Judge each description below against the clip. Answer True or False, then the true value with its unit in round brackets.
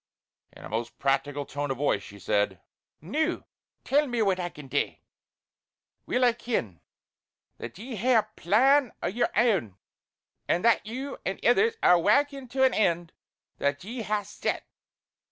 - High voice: True (205 Hz)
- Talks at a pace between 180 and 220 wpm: False (160 wpm)